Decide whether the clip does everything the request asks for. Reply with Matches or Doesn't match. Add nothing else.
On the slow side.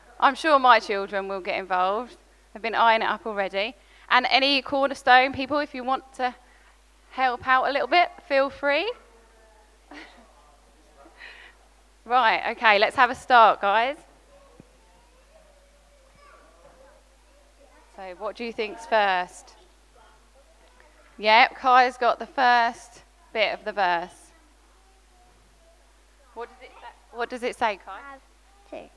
Matches